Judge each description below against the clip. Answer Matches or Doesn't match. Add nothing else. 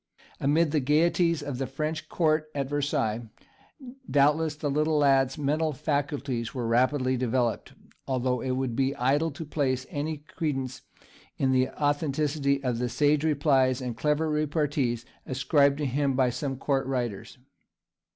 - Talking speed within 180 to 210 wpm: Doesn't match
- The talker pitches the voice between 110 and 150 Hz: Matches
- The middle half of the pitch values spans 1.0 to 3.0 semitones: Matches